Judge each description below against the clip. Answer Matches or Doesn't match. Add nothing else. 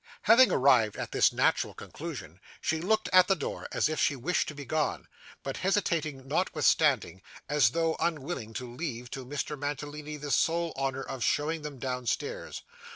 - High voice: Doesn't match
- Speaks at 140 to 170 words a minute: Matches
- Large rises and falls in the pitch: Doesn't match